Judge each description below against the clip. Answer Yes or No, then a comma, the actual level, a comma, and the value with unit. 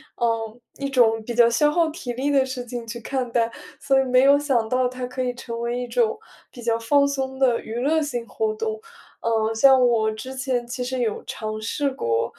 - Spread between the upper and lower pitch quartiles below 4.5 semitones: Yes, average, 2.8 semitones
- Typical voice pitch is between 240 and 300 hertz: Yes, very high, 250 Hz